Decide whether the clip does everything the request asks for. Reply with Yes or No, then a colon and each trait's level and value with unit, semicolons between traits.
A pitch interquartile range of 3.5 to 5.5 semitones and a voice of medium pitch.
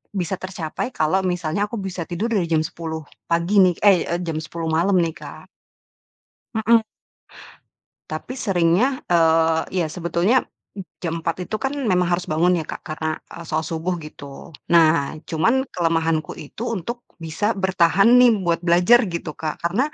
No: average, 2.8 semitones; medium, 170 Hz